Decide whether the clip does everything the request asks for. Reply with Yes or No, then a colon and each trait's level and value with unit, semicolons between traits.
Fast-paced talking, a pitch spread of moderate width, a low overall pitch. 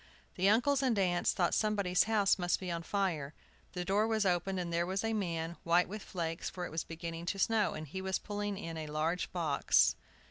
No: fast, 215 wpm; average, 3.4 semitones; medium, 180 Hz